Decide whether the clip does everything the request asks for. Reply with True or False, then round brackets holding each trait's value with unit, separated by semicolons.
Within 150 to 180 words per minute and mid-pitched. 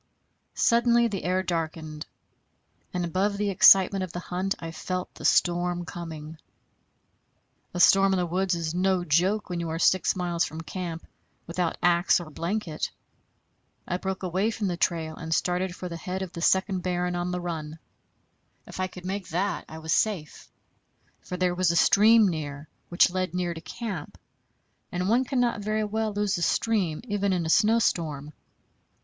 True (175 wpm; 180 Hz)